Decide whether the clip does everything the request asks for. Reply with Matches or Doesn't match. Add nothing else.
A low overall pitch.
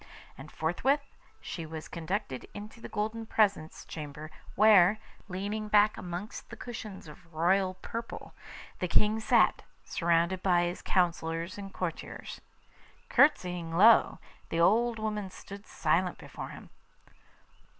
Doesn't match